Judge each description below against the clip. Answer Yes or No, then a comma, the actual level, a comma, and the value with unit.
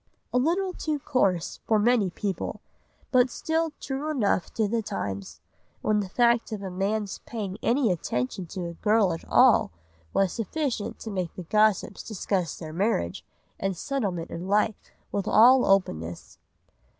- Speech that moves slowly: No, average, 155 wpm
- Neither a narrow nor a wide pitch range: Yes, average, 4.8 semitones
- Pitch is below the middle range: No, high, 205 Hz